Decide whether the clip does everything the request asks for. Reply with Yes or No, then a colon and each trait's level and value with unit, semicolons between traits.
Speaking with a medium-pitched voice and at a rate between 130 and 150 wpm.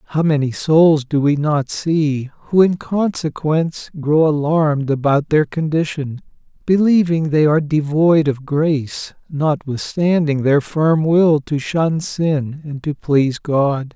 Yes: medium, 150 Hz; average, 140 wpm